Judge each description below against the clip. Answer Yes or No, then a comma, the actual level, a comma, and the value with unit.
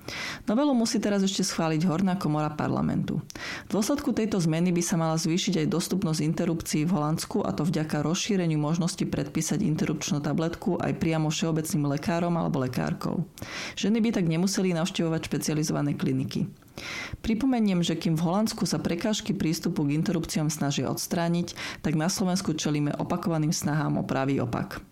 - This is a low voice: No, medium, 170 Hz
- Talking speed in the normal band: Yes, average, 150 wpm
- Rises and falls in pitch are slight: No, average, 3.2 semitones